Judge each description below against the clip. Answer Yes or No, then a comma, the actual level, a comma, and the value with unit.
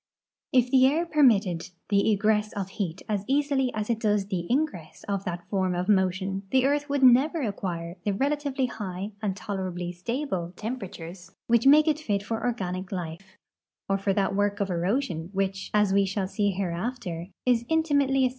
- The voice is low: No, high, 205 Hz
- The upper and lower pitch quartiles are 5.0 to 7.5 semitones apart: Yes, average, 5.3 semitones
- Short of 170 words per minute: No, average, 180 wpm